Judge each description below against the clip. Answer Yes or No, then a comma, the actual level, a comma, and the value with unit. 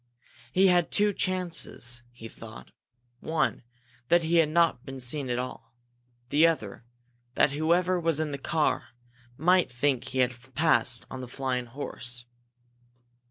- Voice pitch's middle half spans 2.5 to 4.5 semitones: No, average, 5.2 semitones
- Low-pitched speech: No, medium, 145 Hz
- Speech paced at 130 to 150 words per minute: Yes, average, 145 wpm